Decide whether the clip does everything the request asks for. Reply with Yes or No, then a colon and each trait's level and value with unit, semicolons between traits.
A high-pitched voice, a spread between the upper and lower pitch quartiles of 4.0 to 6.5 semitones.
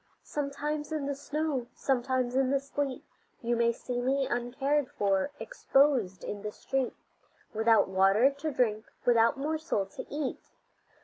No: very high, 260 Hz; average, 3.5 semitones